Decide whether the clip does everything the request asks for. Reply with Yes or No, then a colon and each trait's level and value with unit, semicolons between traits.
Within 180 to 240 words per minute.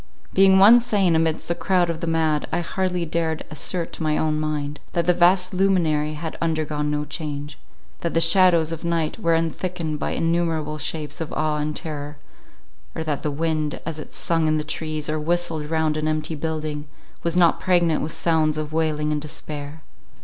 Yes: average, 185 wpm